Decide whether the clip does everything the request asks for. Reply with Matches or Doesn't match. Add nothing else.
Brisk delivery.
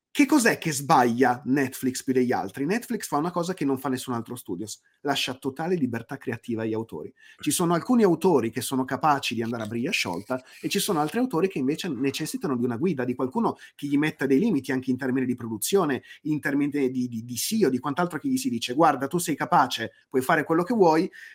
Matches